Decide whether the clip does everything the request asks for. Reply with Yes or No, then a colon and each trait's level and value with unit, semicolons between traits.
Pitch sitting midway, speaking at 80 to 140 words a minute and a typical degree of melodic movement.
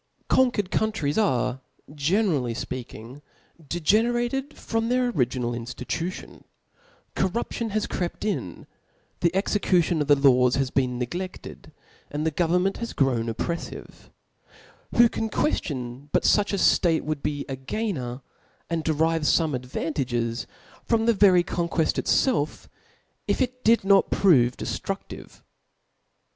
No: medium, 165 Hz; slow, 135 wpm; wide, 8.2 semitones